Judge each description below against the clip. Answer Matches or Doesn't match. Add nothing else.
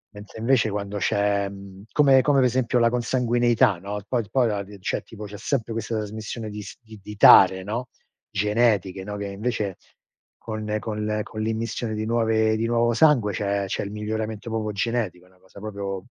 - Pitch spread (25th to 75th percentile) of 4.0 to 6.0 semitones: Doesn't match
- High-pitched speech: Doesn't match